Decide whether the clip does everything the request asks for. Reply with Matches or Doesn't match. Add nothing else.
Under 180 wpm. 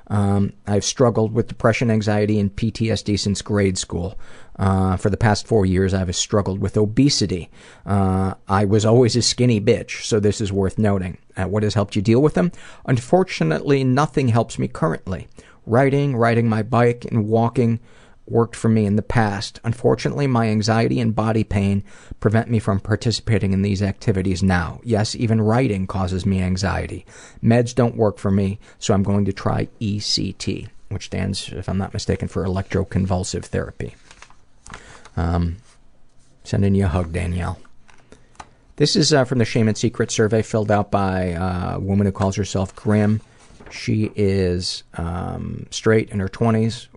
Matches